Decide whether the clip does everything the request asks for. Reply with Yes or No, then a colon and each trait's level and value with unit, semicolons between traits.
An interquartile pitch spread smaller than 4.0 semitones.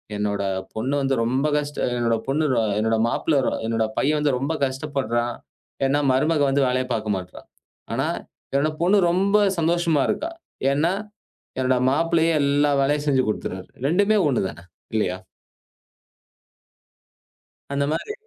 No: average, 4.6 semitones